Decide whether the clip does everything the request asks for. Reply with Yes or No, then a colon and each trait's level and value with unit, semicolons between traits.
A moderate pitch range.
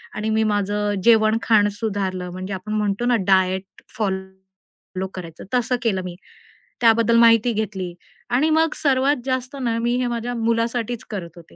Yes: average, 3.8 semitones